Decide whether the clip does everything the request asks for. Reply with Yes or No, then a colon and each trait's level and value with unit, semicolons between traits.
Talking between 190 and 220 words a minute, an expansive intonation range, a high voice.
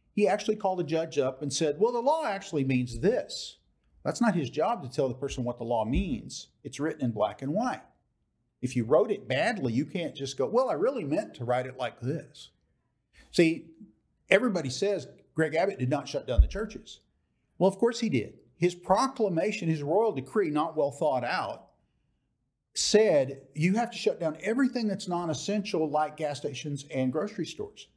No: average, 195 wpm; wide, 6.8 semitones; medium, 160 Hz